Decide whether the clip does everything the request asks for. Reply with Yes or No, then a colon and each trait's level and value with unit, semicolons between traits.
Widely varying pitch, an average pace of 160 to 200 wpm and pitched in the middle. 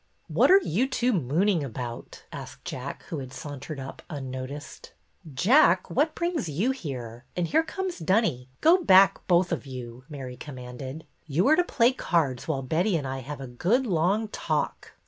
Yes: wide, 8.7 semitones; average, 180 wpm; medium, 160 Hz